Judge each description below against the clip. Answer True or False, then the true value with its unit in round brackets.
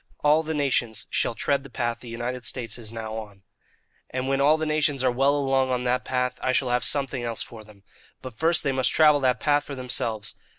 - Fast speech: True (225 wpm)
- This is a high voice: False (130 Hz)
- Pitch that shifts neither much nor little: True (3.1 semitones)